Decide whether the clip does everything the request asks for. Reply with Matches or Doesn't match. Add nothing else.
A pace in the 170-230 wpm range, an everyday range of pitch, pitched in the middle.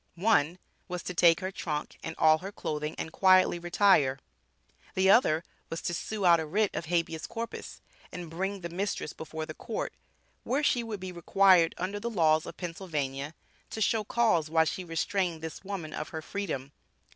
Matches